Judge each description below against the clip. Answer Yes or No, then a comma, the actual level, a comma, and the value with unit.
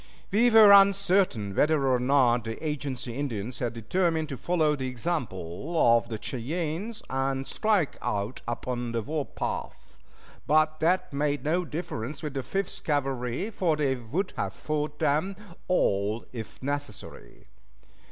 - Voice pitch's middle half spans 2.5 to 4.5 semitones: No, wide, 5.4 semitones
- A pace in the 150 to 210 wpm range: No, average, 140 wpm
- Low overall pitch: No, medium, 145 Hz